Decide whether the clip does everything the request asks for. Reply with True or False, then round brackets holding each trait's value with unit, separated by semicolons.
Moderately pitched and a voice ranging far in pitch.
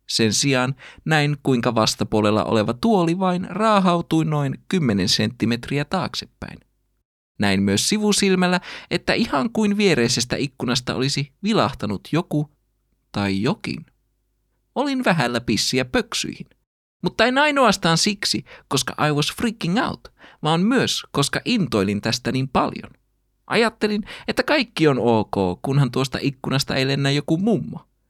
True (145 Hz; 8.4 semitones)